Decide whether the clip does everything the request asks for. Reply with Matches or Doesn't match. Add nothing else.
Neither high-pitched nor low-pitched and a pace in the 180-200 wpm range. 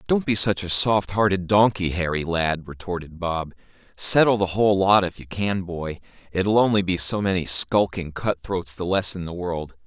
Doesn't match